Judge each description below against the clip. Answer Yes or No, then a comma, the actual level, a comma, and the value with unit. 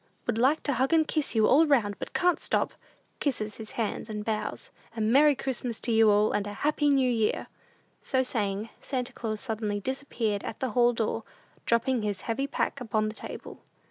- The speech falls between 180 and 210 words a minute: Yes, average, 195 wpm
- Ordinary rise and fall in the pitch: Yes, average, 3.7 semitones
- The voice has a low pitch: No, high, 230 Hz